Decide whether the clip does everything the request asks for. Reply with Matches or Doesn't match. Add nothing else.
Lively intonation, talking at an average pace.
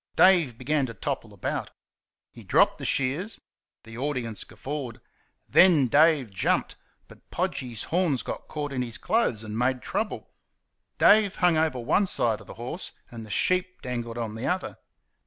Matches